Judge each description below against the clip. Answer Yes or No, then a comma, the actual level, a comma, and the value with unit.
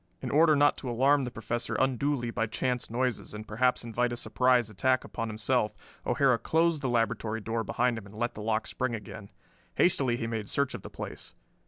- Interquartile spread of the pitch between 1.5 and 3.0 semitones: Yes, narrow, 2.6 semitones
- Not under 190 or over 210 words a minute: Yes, average, 200 wpm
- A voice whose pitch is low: Yes, low, 120 Hz